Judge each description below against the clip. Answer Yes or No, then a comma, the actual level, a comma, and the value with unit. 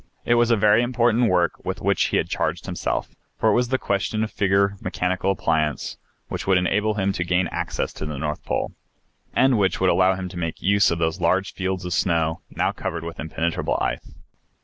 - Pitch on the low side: Yes, very low, 95 Hz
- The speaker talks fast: Yes, fast, 210 wpm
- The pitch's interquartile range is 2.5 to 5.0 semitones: Yes, average, 3.5 semitones